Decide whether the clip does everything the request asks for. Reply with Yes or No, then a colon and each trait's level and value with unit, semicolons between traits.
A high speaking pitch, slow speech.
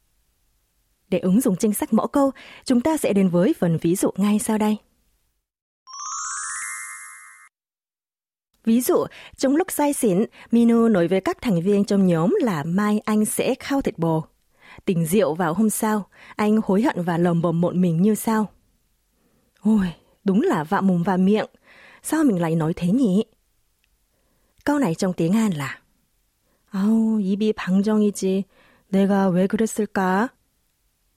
Yes: high, 205 Hz; slow, 155 wpm